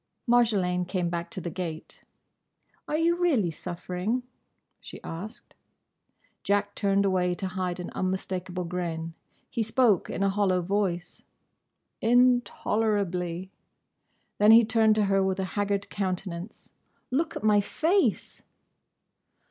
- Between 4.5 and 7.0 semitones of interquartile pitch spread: No, average, 3.4 semitones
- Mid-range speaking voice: No, high, 195 Hz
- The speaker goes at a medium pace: No, slow, 125 wpm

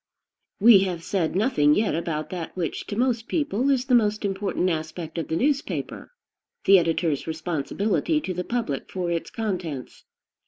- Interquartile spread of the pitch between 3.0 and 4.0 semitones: No, wide, 5.4 semitones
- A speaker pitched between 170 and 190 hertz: Yes, medium, 185 Hz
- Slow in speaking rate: No, average, 160 wpm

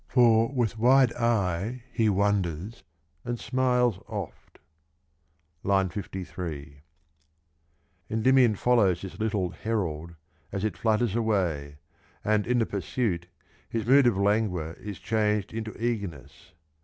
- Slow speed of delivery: Yes, slow, 115 wpm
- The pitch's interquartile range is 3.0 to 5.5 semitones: Yes, average, 4.2 semitones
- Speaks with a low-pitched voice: Yes, low, 105 Hz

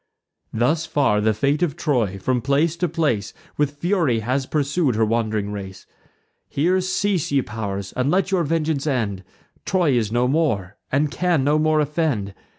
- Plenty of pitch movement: Yes, wide, 6.4 semitones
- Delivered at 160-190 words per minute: Yes, average, 165 wpm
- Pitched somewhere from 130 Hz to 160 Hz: Yes, medium, 140 Hz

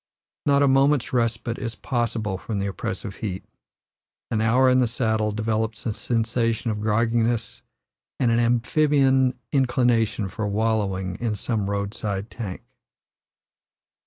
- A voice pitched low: Yes, low, 115 Hz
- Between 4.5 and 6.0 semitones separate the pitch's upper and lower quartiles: No, narrow, 2.5 semitones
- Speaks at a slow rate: Yes, slow, 130 wpm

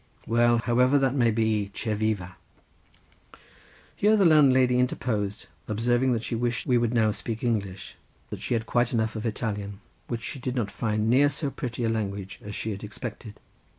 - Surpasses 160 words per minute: Yes, average, 185 wpm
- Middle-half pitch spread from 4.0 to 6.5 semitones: No, average, 2.7 semitones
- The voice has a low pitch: Yes, low, 115 Hz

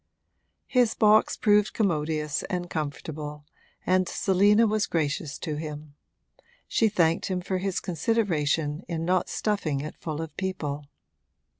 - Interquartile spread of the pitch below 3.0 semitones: No, average, 4.7 semitones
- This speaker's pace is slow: Yes, slow, 130 wpm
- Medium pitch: Yes, medium, 170 Hz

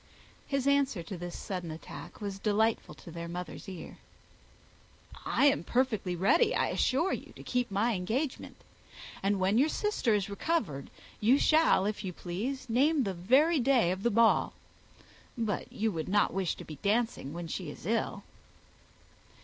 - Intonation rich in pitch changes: Yes, wide, 6.2 semitones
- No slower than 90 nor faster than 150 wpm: No, average, 165 wpm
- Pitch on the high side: Yes, high, 210 Hz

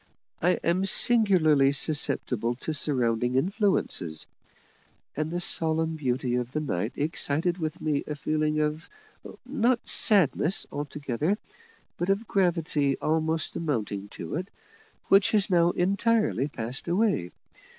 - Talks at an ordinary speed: No, slow, 120 wpm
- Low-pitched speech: No, medium, 155 Hz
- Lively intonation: No, average, 4.9 semitones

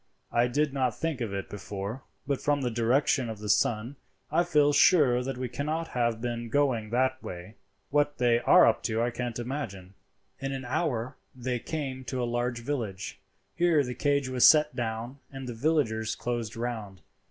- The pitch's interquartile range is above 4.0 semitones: No, average, 3.6 semitones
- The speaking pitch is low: Yes, low, 125 Hz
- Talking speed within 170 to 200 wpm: Yes, average, 185 wpm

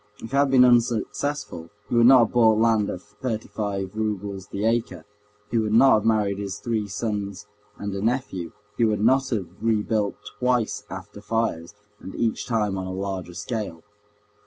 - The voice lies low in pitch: Yes, low, 105 Hz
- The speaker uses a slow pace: No, average, 180 wpm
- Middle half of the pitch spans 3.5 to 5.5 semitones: No, average, 2.9 semitones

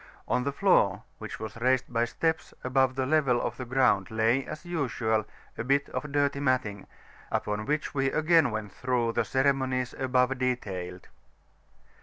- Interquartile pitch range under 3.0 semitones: No, average, 3.4 semitones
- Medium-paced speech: Yes, average, 160 wpm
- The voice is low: Yes, low, 130 Hz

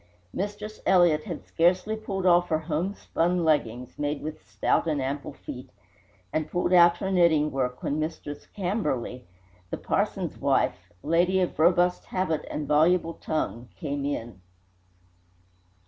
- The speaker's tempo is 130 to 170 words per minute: Yes, average, 140 wpm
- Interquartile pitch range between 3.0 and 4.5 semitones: Yes, average, 3.5 semitones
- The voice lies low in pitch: No, medium, 165 Hz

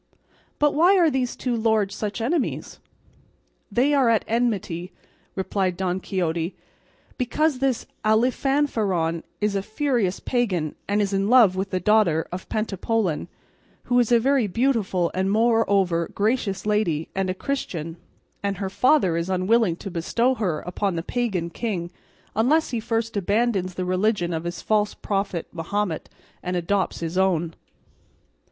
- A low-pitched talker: No, high, 200 Hz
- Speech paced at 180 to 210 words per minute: No, average, 145 wpm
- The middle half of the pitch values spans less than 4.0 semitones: No, average, 4.5 semitones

